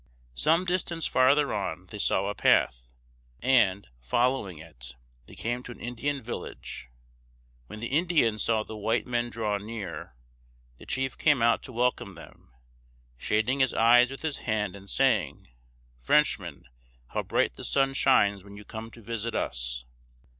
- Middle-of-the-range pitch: No, low, 115 Hz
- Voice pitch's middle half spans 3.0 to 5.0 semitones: Yes, average, 4.4 semitones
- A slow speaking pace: No, average, 155 wpm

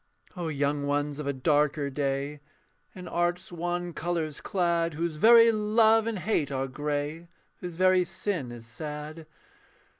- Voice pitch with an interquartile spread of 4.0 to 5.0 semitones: No, average, 3.6 semitones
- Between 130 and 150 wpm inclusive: Yes, average, 145 wpm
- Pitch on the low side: No, medium, 160 Hz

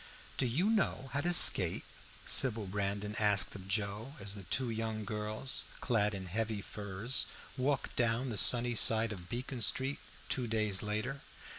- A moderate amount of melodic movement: Yes, average, 3.7 semitones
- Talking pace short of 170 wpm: Yes, average, 160 wpm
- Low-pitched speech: Yes, low, 110 Hz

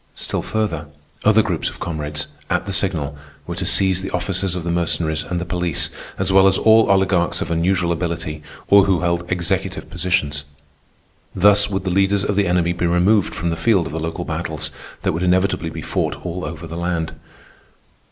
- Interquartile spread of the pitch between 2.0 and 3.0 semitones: Yes, narrow, 2.4 semitones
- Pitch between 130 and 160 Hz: No, very low, 90 Hz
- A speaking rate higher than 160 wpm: Yes, average, 190 wpm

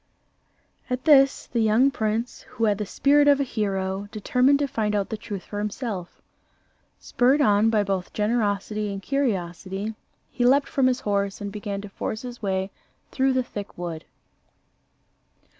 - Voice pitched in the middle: No, high, 215 Hz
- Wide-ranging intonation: No, average, 4.0 semitones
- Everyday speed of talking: Yes, average, 160 wpm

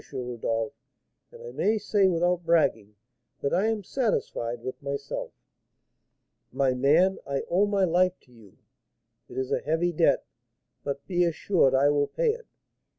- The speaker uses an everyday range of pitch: No, wide, 6.2 semitones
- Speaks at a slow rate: No, average, 150 wpm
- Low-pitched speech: No, medium, 165 Hz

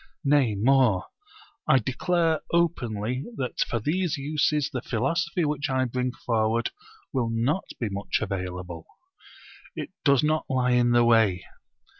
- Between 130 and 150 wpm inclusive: Yes, slow, 135 wpm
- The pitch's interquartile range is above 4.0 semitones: Yes, average, 4.7 semitones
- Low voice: Yes, low, 125 Hz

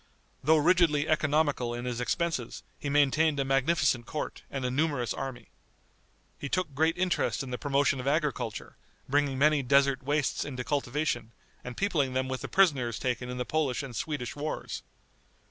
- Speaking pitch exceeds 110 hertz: Yes, medium, 140 Hz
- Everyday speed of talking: Yes, average, 165 wpm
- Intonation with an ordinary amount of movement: Yes, average, 3.3 semitones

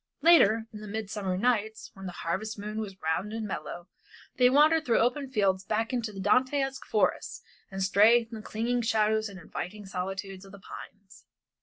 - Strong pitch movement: No, average, 3.2 semitones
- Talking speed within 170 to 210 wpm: Yes, average, 185 wpm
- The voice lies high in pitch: Yes, high, 215 Hz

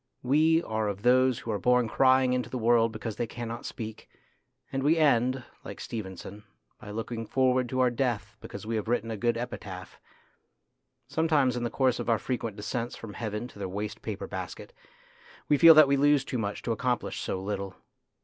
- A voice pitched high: No, low, 120 Hz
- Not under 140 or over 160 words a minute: No, average, 195 wpm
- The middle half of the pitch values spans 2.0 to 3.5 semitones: Yes, average, 3.2 semitones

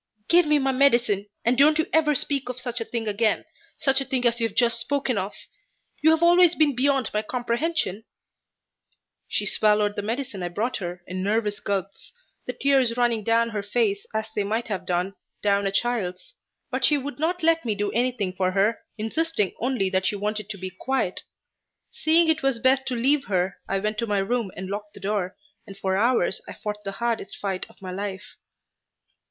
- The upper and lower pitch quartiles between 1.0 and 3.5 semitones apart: No, average, 4.8 semitones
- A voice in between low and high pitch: No, high, 225 Hz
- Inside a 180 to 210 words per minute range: Yes, average, 200 wpm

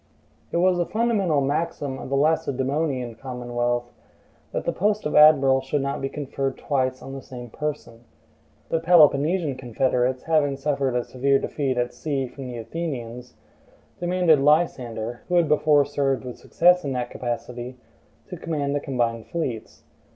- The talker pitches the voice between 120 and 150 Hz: Yes, low, 135 Hz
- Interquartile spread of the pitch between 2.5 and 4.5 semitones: Yes, average, 3.8 semitones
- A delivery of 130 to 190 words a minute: Yes, average, 155 wpm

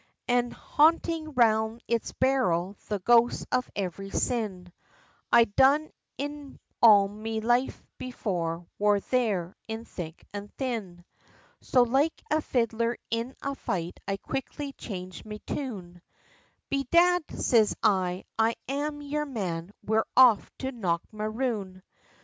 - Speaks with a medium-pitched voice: No, high, 225 Hz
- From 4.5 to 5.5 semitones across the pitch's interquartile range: Yes, average, 5.1 semitones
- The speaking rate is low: Yes, slow, 125 wpm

